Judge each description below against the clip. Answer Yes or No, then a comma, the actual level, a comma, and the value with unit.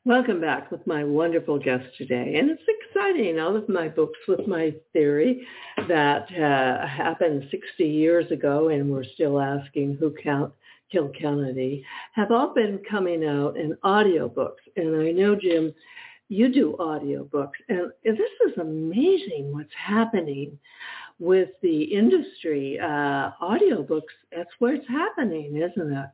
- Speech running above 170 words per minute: No, average, 140 wpm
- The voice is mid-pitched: Yes, medium, 165 Hz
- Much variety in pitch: Yes, wide, 7.3 semitones